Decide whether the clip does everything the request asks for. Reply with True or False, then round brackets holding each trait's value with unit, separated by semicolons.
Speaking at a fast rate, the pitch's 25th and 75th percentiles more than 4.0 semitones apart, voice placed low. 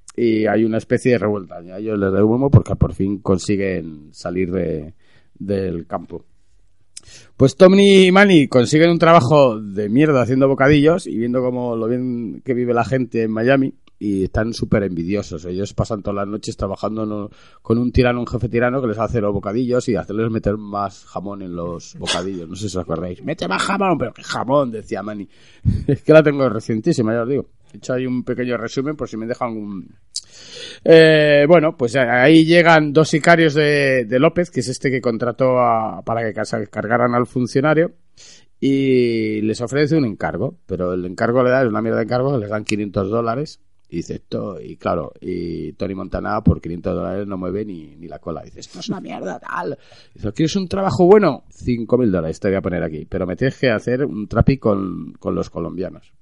True (200 wpm; 4.6 semitones; 115 Hz)